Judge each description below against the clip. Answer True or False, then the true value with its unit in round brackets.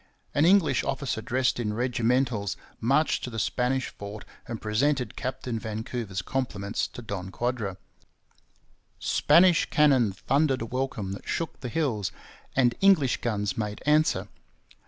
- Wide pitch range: False (4.2 semitones)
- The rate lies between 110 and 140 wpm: True (135 wpm)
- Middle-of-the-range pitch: False (120 Hz)